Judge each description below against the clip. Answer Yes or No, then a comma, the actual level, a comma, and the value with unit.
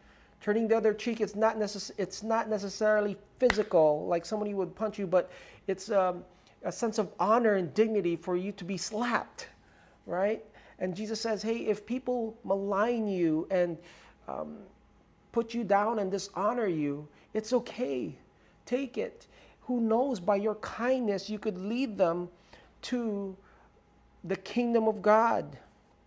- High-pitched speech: Yes, high, 210 Hz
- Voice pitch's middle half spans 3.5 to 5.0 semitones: No, average, 3.0 semitones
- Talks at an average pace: Yes, average, 150 wpm